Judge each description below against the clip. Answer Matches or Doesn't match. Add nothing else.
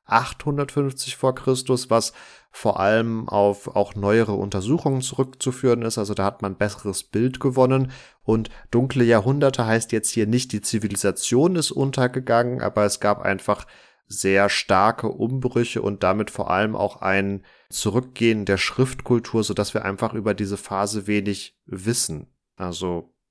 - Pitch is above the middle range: Doesn't match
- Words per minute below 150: Matches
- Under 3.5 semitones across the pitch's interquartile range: Doesn't match